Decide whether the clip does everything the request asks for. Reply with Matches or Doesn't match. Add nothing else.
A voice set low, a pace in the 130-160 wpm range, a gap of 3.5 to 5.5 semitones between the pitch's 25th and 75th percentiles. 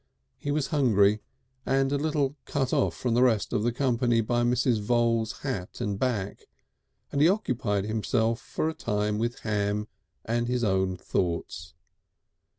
Matches